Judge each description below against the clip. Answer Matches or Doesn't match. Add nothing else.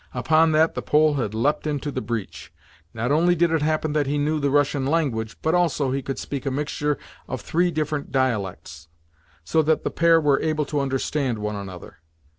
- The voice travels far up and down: Doesn't match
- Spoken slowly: Doesn't match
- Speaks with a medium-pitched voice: Matches